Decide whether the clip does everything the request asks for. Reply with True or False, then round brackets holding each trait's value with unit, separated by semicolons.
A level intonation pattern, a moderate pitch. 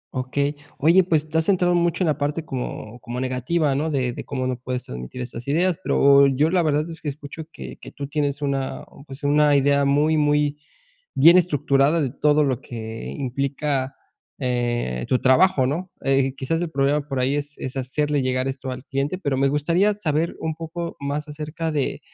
False (3.0 semitones; 145 Hz)